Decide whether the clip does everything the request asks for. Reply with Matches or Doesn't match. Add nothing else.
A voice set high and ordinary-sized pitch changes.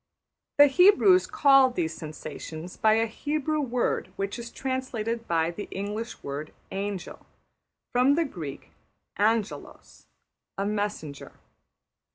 Doesn't match